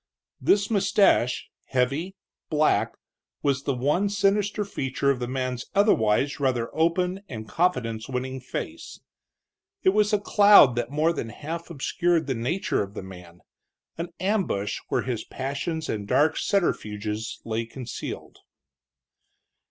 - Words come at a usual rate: No, slow, 130 wpm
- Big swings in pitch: Yes, wide, 7.0 semitones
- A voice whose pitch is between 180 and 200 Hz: No, medium, 140 Hz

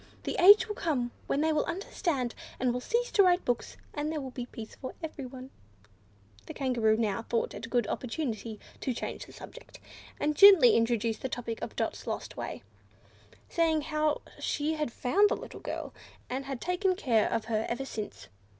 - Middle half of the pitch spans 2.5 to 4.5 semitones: No, average, 5.3 semitones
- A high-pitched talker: Yes, very high, 260 Hz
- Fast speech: No, average, 185 wpm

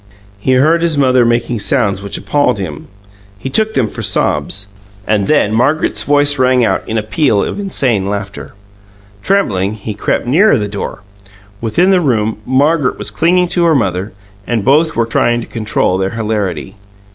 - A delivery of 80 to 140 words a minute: No, average, 170 wpm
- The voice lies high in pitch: No, low, 120 Hz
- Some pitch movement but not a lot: No, wide, 6.1 semitones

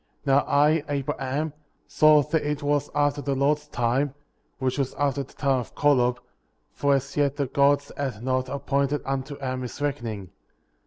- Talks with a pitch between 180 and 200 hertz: No, medium, 140 Hz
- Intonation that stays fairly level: Yes, narrow, 1.7 semitones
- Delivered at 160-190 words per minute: Yes, average, 165 wpm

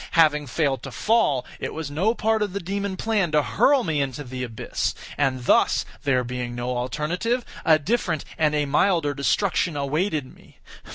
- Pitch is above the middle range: No, medium, 150 Hz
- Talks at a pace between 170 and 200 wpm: Yes, average, 175 wpm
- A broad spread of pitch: Yes, wide, 6.2 semitones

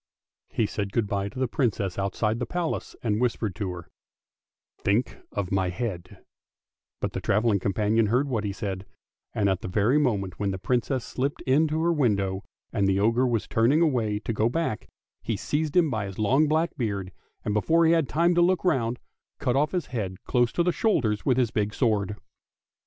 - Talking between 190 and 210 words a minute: Yes, average, 200 wpm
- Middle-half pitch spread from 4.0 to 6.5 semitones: Yes, wide, 5.5 semitones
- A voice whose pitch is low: Yes, low, 115 Hz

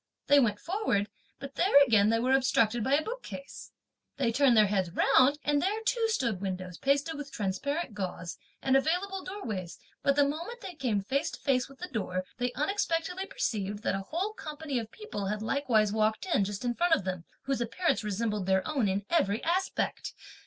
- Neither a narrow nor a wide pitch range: No, wide, 7.4 semitones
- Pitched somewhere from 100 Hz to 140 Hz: No, very high, 260 Hz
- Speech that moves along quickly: No, average, 195 wpm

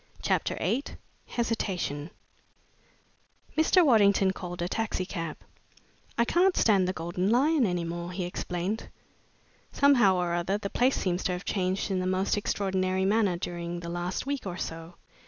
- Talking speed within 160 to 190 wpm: No, average, 150 wpm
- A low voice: No, medium, 185 Hz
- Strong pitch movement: No, average, 3.9 semitones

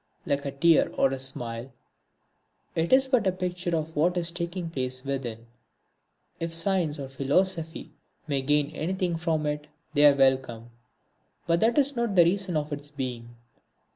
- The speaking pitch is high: No, medium, 155 Hz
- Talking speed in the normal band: Yes, average, 165 wpm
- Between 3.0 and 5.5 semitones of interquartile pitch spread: Yes, average, 4.6 semitones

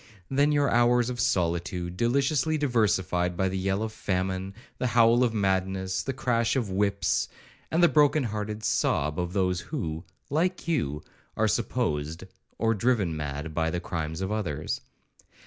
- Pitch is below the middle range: Yes, low, 100 Hz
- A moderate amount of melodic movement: No, wide, 5.7 semitones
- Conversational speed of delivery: Yes, average, 155 wpm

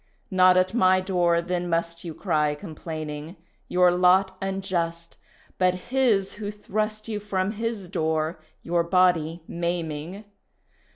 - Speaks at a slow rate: Yes, slow, 125 wpm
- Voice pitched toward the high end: No, medium, 180 Hz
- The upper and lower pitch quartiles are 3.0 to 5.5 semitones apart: No, narrow, 2.5 semitones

